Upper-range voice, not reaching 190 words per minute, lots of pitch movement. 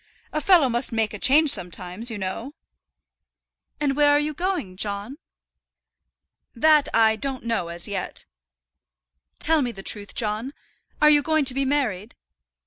Yes: very high, 250 Hz; average, 150 wpm; wide, 5.8 semitones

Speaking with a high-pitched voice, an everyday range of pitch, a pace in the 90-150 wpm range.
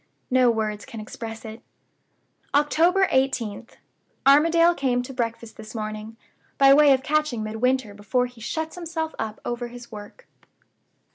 Yes: high, 245 Hz; average, 4.6 semitones; average, 140 wpm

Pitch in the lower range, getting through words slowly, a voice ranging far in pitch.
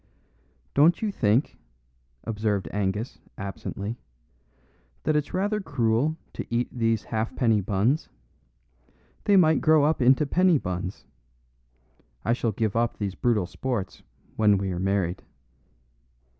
Yes: low, 115 Hz; slow, 120 wpm; wide, 6.4 semitones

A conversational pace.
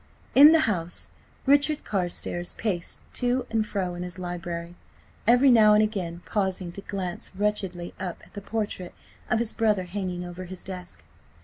Yes: average, 165 wpm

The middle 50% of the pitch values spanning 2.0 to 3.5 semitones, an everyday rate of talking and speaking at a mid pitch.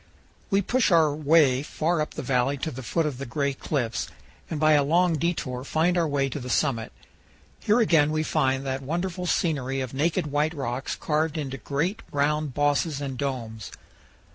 Yes: average, 3.1 semitones; average, 185 wpm; medium, 145 Hz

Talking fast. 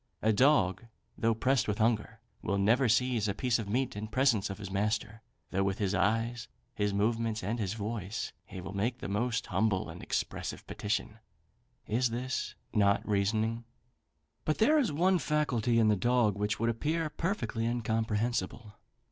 No: average, 165 wpm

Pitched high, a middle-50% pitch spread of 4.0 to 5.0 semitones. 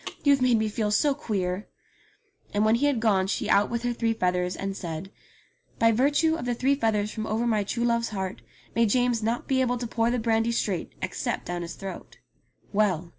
No: high, 225 Hz; average, 3.5 semitones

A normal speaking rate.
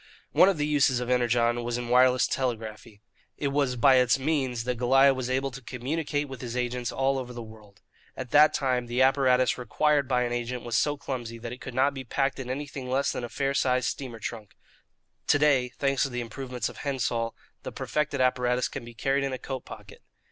No: fast, 215 wpm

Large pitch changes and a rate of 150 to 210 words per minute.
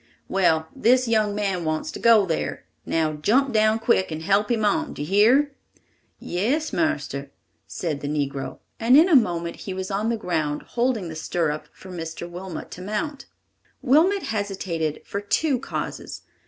Yes: wide, 6.3 semitones; average, 170 wpm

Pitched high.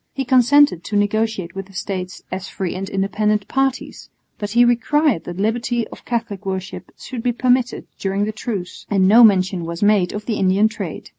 Yes: high, 210 Hz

